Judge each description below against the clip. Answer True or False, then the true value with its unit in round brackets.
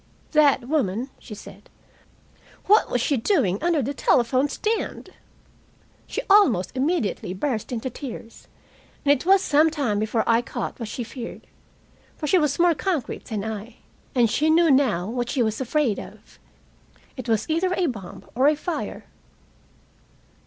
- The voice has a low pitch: False (260 Hz)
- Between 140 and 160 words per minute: True (150 wpm)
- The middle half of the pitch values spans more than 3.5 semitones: True (5.4 semitones)